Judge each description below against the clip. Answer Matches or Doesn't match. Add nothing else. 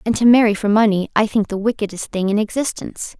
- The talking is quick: Matches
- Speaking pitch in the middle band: Doesn't match